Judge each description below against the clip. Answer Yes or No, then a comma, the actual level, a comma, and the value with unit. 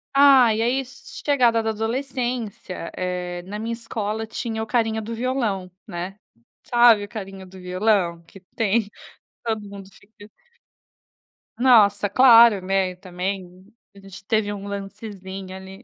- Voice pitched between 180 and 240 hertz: Yes, high, 205 Hz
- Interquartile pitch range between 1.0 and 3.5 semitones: Yes, average, 3.2 semitones